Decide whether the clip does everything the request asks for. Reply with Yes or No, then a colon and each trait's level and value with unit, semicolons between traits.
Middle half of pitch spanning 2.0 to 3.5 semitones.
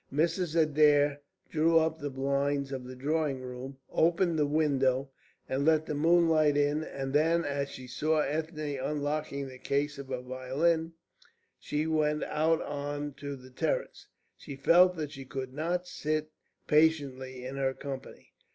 Yes: average, 2.7 semitones